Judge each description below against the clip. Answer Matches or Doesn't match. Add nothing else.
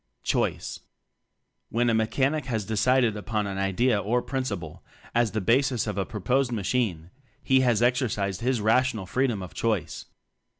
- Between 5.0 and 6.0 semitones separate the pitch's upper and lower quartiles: Doesn't match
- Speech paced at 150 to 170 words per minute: Matches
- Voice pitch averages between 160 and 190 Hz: Doesn't match